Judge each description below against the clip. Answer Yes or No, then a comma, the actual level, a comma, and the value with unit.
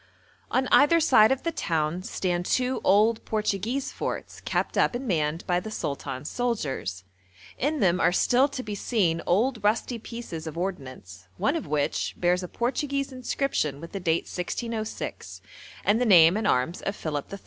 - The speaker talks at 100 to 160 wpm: No, average, 170 wpm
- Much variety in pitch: Yes, wide, 6.9 semitones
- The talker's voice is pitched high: Yes, high, 200 Hz